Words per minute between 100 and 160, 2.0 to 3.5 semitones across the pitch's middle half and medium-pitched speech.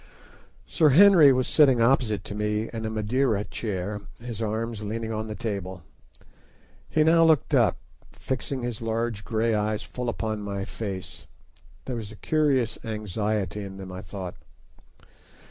No: average, 150 wpm; average, 3.0 semitones; low, 110 Hz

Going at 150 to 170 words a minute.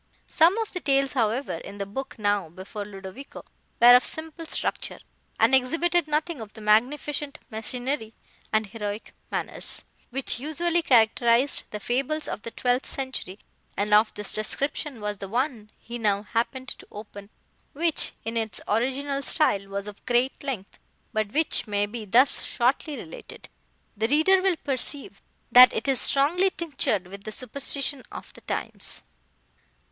Yes: average, 155 wpm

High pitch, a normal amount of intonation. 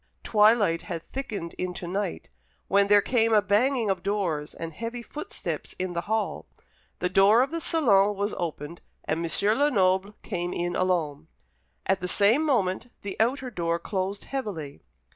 Yes: high, 200 Hz; average, 4.3 semitones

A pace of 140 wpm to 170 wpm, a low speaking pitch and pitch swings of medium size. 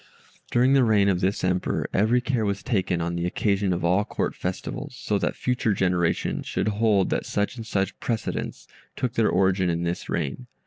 No: average, 190 wpm; low, 100 Hz; average, 3.8 semitones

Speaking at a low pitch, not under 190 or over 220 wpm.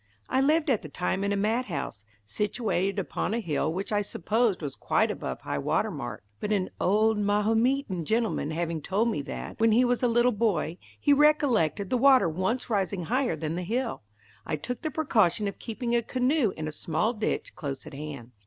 No: high, 210 Hz; average, 200 wpm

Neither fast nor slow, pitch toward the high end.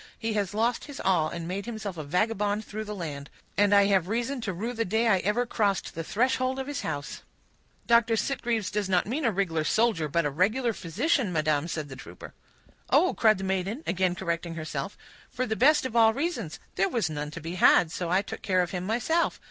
No: fast, 220 wpm; high, 200 Hz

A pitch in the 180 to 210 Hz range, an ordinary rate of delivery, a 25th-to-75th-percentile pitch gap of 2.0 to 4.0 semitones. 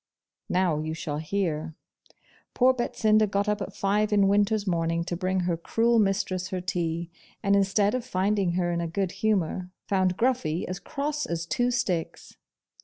Yes: high, 190 Hz; average, 170 wpm; average, 3.6 semitones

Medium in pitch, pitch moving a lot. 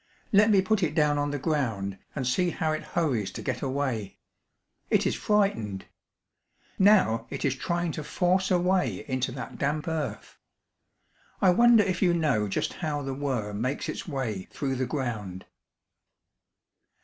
Yes: medium, 145 Hz; wide, 6.1 semitones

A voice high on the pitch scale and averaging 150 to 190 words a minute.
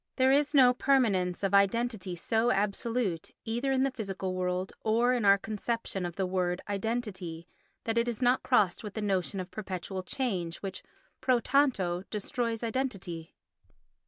Yes: high, 210 Hz; average, 160 wpm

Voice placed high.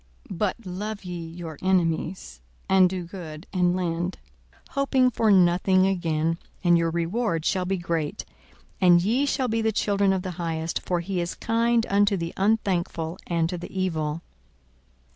No: medium, 180 Hz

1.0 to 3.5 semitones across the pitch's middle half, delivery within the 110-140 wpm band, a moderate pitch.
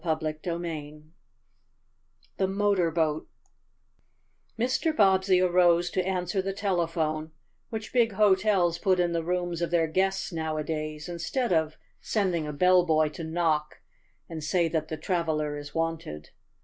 Yes: average, 3.1 semitones; slow, 135 wpm; medium, 170 Hz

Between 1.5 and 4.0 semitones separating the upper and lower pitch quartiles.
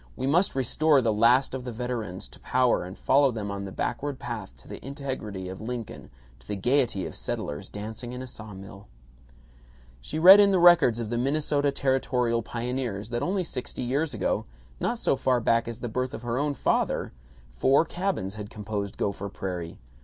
No: average, 4.7 semitones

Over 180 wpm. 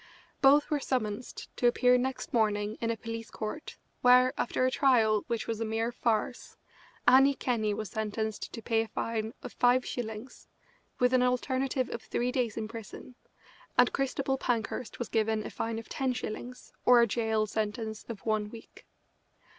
No: average, 170 wpm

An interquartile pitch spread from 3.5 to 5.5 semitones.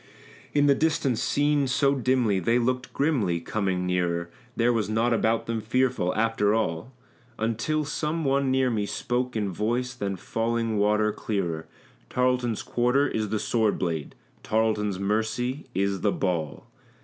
Yes: average, 3.8 semitones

